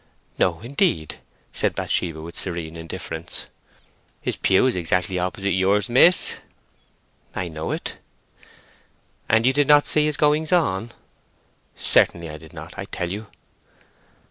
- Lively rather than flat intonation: Yes, wide, 7.6 semitones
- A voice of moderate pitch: No, very low, 95 Hz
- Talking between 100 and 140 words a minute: Yes, slow, 135 wpm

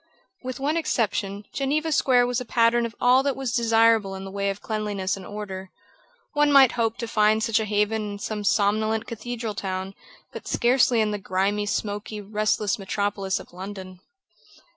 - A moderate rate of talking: Yes, average, 175 wpm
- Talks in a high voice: Yes, high, 215 Hz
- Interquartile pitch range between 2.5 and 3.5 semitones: Yes, average, 2.8 semitones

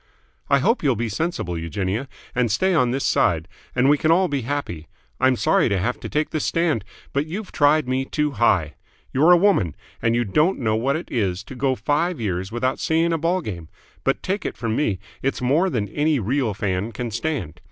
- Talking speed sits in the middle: No, fast, 215 wpm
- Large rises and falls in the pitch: Yes, wide, 6.6 semitones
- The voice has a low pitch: Yes, low, 130 Hz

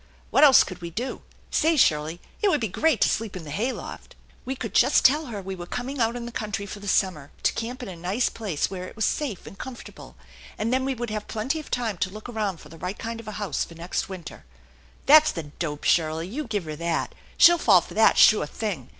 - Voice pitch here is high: Yes, high, 210 Hz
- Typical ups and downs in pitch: No, wide, 5.8 semitones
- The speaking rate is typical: No, fast, 260 wpm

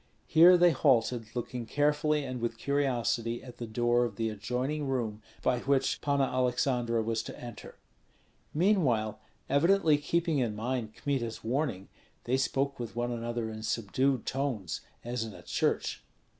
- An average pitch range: Yes, average, 3.4 semitones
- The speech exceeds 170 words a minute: No, average, 150 wpm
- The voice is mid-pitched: No, low, 125 Hz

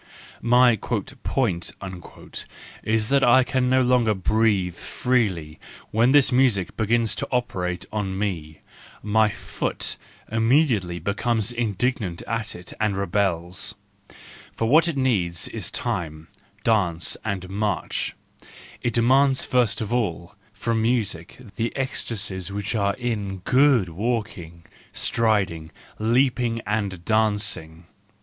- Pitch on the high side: No, low, 110 Hz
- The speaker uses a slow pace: Yes, slow, 115 wpm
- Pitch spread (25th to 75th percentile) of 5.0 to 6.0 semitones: No, average, 4.5 semitones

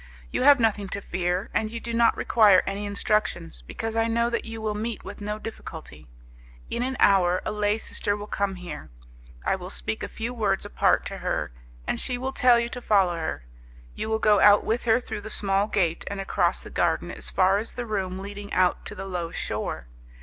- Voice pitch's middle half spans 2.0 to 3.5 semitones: Yes, average, 2.8 semitones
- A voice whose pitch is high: Yes, high, 205 Hz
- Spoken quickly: Yes, fast, 215 wpm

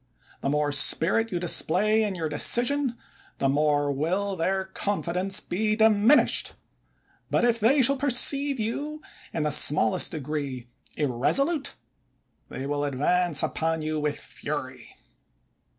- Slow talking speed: Yes, slow, 125 wpm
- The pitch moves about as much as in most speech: No, wide, 7.3 semitones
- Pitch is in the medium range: Yes, medium, 180 Hz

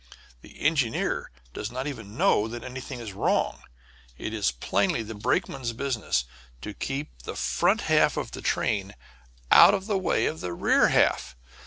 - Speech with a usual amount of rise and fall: Yes, average, 4.9 semitones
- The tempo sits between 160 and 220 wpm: Yes, average, 165 wpm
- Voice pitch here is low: Yes, low, 115 Hz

